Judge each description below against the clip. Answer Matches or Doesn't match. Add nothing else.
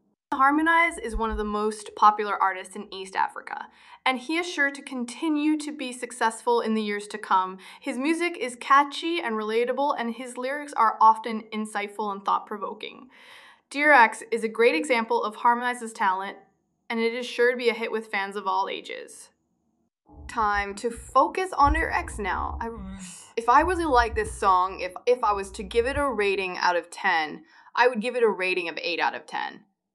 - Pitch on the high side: Matches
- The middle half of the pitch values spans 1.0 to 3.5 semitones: Doesn't match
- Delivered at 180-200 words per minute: Matches